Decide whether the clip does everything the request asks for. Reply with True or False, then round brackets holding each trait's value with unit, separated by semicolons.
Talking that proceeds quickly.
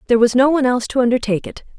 True (270 wpm)